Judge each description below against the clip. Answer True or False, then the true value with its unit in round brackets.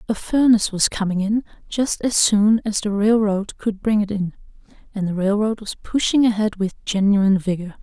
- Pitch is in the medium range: False (210 Hz)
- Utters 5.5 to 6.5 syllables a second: False (5.1 syllables/s)